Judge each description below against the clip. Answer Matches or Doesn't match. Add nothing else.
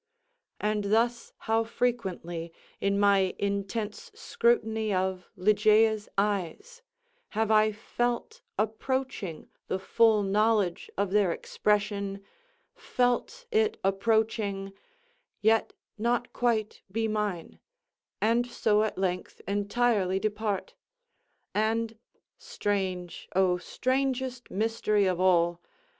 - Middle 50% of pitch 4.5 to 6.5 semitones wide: Doesn't match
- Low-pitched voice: Doesn't match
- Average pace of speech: Doesn't match